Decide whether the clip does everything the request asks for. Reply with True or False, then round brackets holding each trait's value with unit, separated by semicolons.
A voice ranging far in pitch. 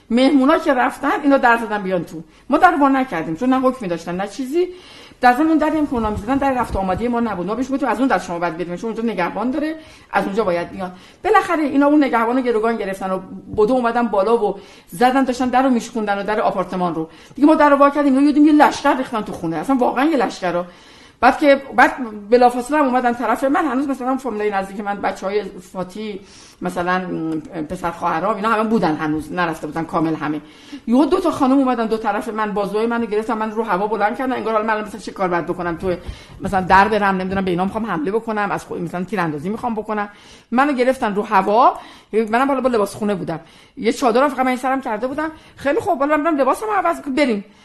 True (6.0 semitones)